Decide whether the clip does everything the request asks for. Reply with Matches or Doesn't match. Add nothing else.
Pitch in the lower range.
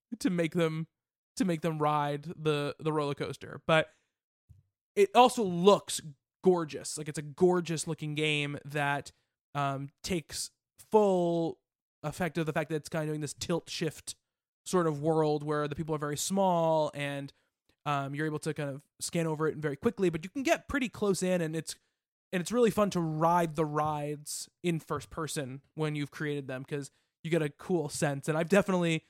Doesn't match